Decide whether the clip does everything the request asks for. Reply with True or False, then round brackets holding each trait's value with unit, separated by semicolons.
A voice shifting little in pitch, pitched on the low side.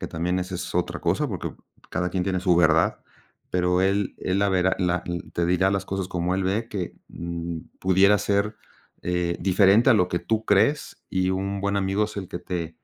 True (1.9 semitones; 95 Hz)